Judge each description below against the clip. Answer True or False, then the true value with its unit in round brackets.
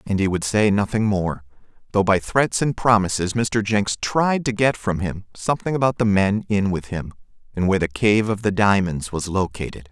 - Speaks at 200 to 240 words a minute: True (205 wpm)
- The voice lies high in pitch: False (105 Hz)